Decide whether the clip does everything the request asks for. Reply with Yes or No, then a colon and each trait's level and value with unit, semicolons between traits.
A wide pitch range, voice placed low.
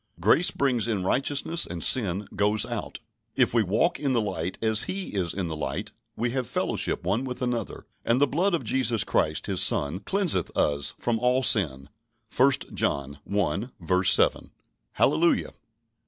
Yes: wide, 6.0 semitones; low, 110 Hz